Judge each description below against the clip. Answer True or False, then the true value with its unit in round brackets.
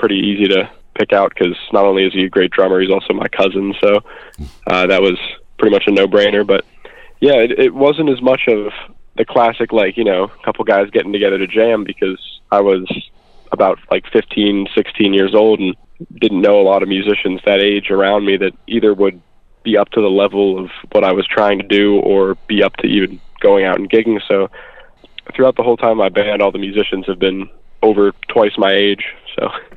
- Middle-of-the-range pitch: False (100 Hz)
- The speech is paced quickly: True (215 wpm)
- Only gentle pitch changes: True (1.8 semitones)